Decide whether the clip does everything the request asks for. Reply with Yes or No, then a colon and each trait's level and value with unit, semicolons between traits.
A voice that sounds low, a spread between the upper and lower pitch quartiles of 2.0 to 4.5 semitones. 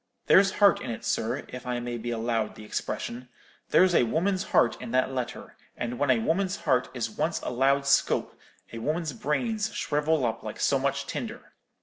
No: low, 130 Hz; average, 5.2 semitones